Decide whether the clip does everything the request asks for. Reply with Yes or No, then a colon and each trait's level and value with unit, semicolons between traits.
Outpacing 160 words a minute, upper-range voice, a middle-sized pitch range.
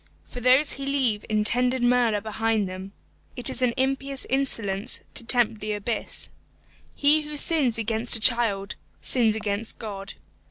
No: average, 150 wpm; high, 235 Hz; average, 3.5 semitones